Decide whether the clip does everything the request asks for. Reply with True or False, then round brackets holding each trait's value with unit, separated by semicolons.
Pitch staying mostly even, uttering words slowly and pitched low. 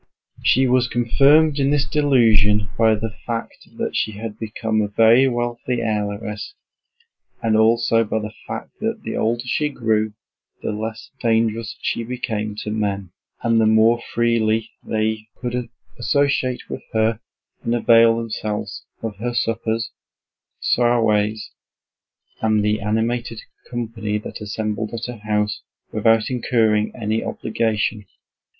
True (1.7 semitones; 130 wpm; 115 Hz)